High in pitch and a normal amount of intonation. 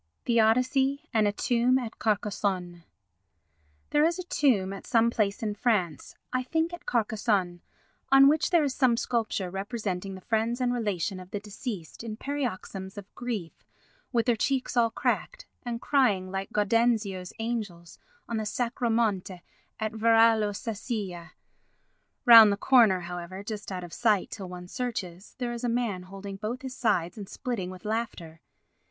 Yes: high, 220 Hz; average, 4.0 semitones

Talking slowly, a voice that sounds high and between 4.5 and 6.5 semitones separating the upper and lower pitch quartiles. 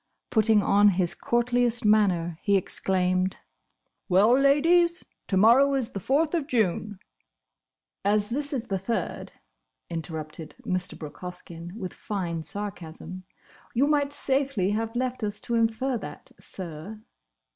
Yes: slow, 130 wpm; high, 210 Hz; average, 5.2 semitones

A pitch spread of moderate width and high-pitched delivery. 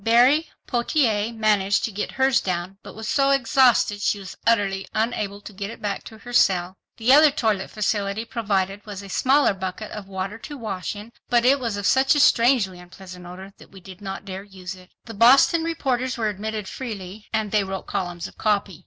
Yes: average, 3.7 semitones; high, 210 Hz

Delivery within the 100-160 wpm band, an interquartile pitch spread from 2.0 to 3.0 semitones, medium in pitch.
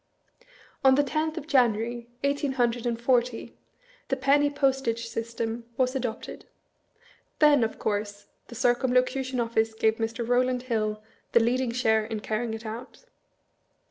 No: average, 140 wpm; narrow, 2.6 semitones; high, 240 Hz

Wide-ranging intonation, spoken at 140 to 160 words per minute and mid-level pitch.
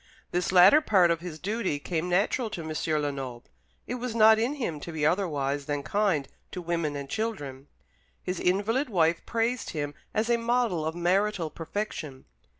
No: wide, 6.1 semitones; average, 170 wpm; medium, 175 Hz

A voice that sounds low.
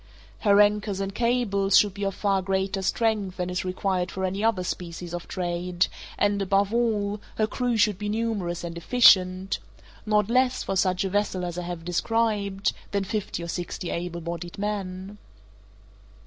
No: high, 195 Hz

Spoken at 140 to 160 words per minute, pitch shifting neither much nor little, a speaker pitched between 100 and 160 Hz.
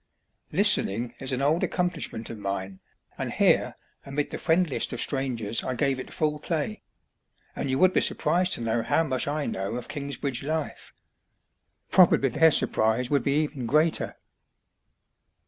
Yes: average, 155 wpm; average, 4.6 semitones; medium, 140 Hz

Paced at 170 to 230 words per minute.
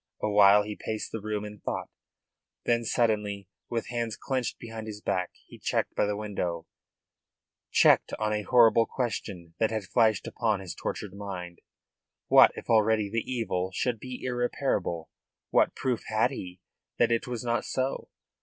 No: average, 160 wpm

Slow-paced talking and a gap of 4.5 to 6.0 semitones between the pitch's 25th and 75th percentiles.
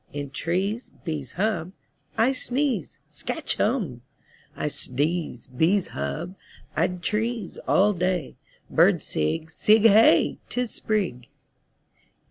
Yes: slow, 105 wpm; wide, 5.4 semitones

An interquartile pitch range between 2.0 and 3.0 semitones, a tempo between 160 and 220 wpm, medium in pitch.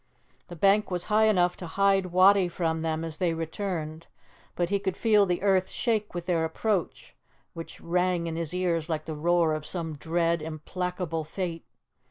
Yes: average, 2.7 semitones; average, 180 wpm; medium, 175 Hz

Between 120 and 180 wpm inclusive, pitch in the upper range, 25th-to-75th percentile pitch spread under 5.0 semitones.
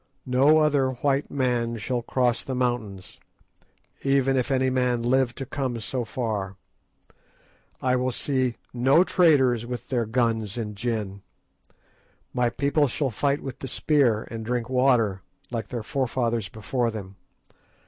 No: average, 140 wpm; low, 125 Hz; narrow, 2.6 semitones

